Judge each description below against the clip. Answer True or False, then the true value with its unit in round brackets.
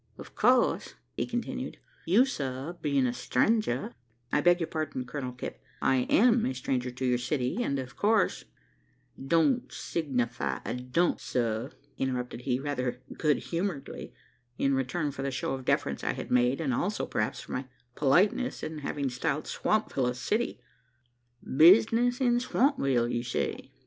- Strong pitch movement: True (5.8 semitones)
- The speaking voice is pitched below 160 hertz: True (135 Hz)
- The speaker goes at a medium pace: True (160 wpm)